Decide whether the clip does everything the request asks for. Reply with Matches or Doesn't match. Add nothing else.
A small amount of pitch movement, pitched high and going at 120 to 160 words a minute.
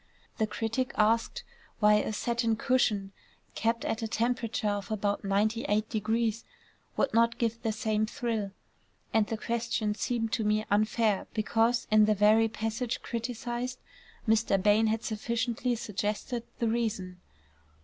Matches